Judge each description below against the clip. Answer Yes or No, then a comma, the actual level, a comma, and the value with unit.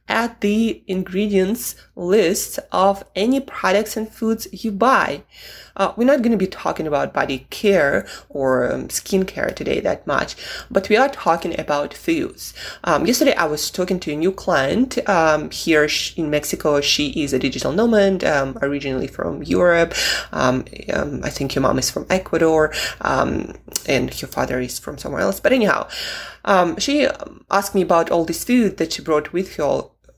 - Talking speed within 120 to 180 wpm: Yes, average, 175 wpm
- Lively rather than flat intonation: Yes, wide, 6.3 semitones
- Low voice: No, high, 190 Hz